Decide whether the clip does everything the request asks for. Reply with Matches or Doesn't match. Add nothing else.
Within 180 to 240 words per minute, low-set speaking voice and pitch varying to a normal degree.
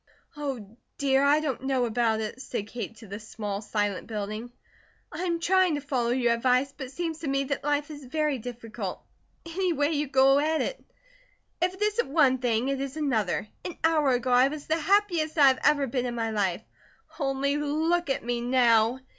Doesn't match